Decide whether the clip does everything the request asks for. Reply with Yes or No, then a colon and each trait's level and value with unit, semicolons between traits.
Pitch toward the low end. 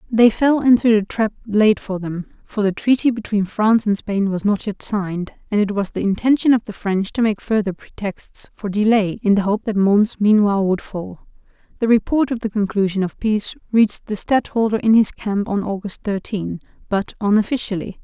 No: high, 210 Hz